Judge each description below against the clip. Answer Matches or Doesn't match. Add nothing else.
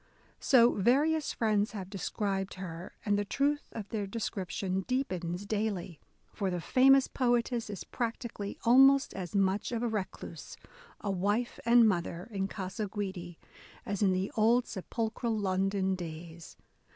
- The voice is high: Matches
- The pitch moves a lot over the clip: Doesn't match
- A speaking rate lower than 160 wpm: Matches